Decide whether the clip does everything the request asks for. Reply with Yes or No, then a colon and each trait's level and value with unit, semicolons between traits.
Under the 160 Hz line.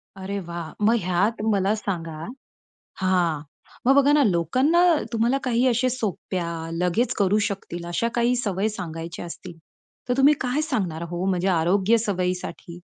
No: high, 195 Hz